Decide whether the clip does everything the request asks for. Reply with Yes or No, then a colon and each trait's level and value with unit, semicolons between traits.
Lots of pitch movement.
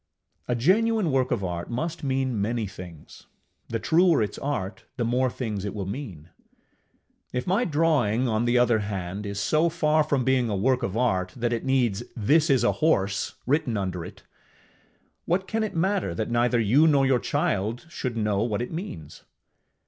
Yes: wide, 6.0 semitones